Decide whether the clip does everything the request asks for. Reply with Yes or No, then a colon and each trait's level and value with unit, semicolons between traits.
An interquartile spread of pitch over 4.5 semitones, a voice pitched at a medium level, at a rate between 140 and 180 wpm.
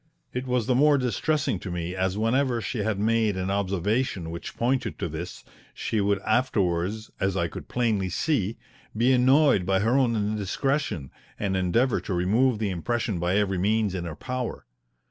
No: average, 4.9 semitones; low, 105 Hz; average, 175 wpm